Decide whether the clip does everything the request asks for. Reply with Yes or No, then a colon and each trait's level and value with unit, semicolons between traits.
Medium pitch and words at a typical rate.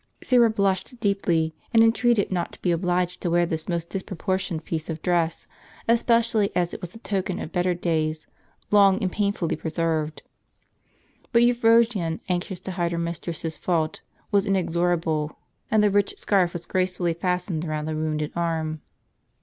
Yes: medium, 175 Hz; average, 160 wpm